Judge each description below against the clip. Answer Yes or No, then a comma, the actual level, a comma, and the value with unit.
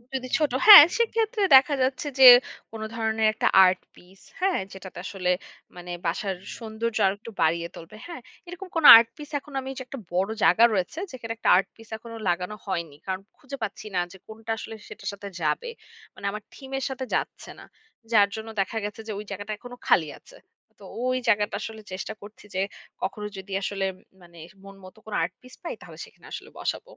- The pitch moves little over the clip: No, average, 5.1 semitones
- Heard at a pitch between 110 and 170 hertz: No, high, 220 Hz